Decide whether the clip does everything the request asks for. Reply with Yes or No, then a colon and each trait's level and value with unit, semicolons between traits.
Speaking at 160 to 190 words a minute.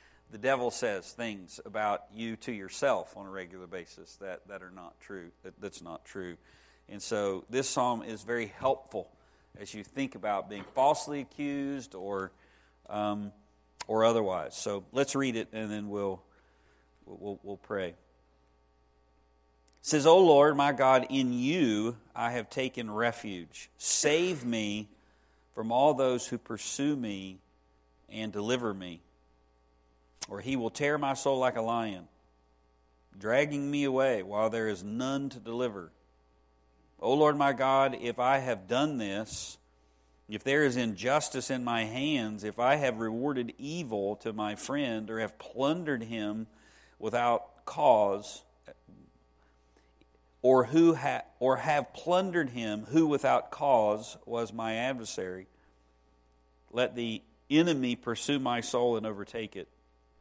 No: average, 145 wpm